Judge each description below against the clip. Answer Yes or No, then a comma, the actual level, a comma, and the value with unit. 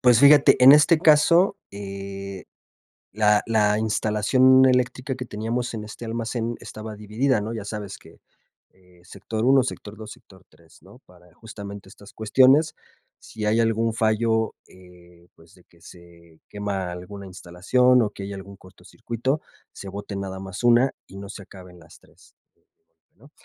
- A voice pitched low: Yes, low, 105 Hz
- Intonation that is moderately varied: Yes, average, 3.6 semitones